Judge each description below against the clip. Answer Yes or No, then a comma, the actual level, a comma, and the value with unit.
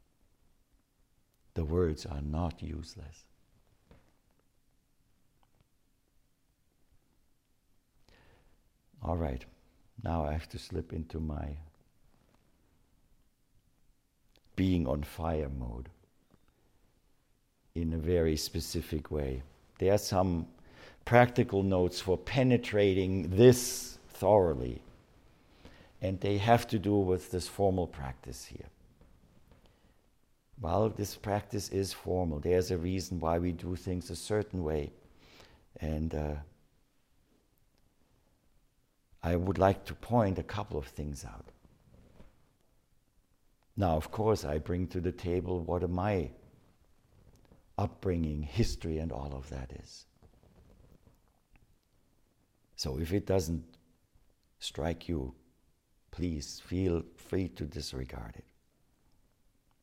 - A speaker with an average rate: No, slow, 100 wpm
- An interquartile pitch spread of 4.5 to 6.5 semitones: No, average, 3.7 semitones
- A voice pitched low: Yes, very low, 85 Hz